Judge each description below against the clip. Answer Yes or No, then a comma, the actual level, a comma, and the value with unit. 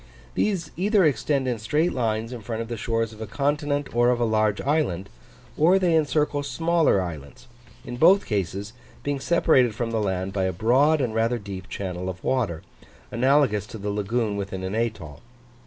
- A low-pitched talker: Yes, low, 115 Hz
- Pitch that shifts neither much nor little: No, wide, 6.0 semitones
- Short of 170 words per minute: No, average, 185 wpm